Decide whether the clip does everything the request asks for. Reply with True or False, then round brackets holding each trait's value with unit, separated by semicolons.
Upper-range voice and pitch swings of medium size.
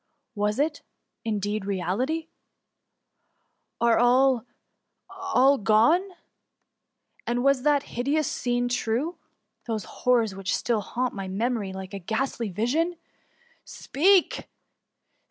True (245 Hz; 4.6 semitones)